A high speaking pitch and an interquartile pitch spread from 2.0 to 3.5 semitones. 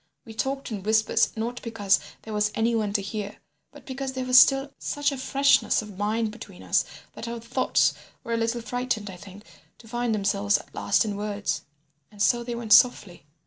Yes: high, 225 Hz; average, 3.0 semitones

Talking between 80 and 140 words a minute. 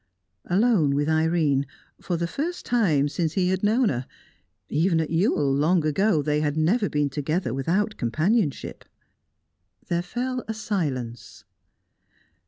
Yes: slow, 135 wpm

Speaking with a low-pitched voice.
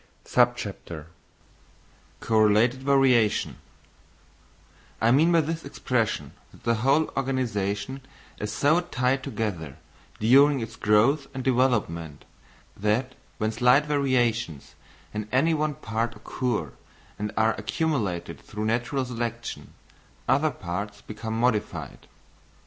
Yes: low, 120 Hz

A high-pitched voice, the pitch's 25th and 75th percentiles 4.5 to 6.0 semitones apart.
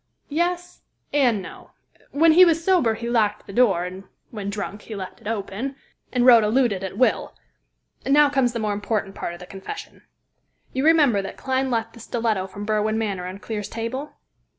Yes: high, 225 Hz; average, 4.8 semitones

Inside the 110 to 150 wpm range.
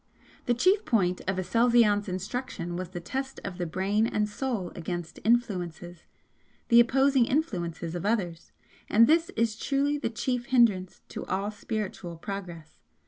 Yes: average, 145 wpm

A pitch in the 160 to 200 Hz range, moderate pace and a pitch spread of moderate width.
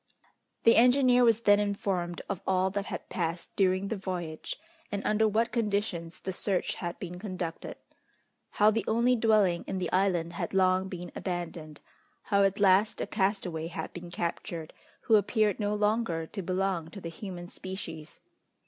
Yes: high, 190 Hz; average, 165 wpm; average, 3.1 semitones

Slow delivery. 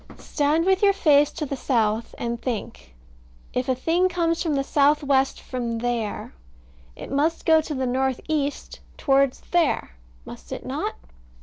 No: average, 165 wpm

